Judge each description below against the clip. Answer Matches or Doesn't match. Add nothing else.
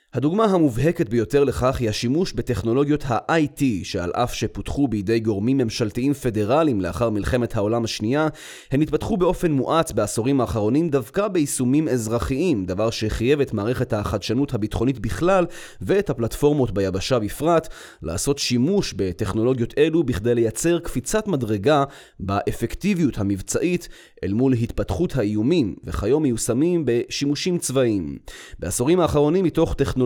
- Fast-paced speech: Doesn't match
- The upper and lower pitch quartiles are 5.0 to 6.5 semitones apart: Matches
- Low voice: Matches